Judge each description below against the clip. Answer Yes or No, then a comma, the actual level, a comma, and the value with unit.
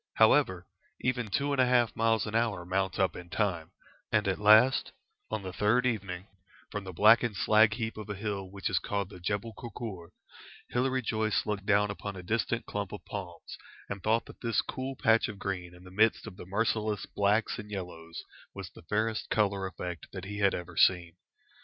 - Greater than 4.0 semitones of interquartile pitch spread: No, average, 3.0 semitones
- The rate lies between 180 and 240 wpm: Yes, average, 195 wpm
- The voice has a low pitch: Yes, low, 105 Hz